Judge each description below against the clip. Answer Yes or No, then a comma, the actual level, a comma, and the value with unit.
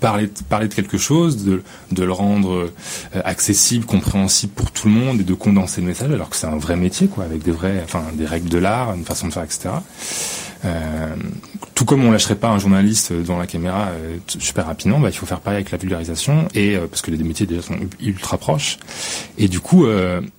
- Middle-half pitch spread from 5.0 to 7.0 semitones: No, average, 3.2 semitones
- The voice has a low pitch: Yes, very low, 95 Hz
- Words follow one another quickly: Yes, fast, 225 wpm